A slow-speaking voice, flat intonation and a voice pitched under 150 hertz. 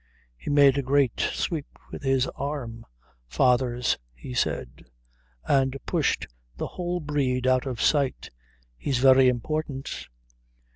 Yes: slow, 125 wpm; narrow, 2.3 semitones; low, 135 Hz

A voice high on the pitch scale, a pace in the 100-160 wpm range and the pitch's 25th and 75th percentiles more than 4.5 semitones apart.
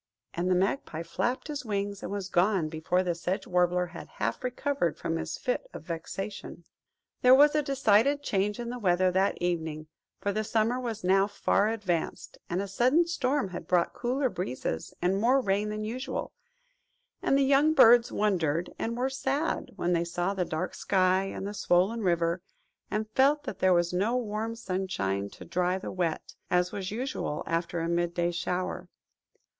No: high, 195 Hz; average, 180 wpm; average, 5.2 semitones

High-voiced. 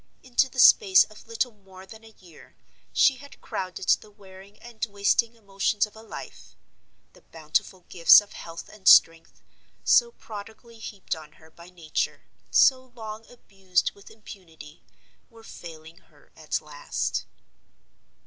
Yes: high, 200 Hz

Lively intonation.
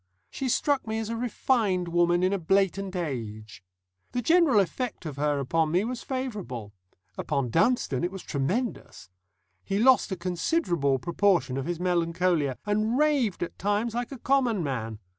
Yes: wide, 7.0 semitones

